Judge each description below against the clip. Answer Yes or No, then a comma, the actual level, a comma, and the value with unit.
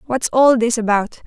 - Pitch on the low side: No, high, 240 Hz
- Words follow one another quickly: No, average, 190 wpm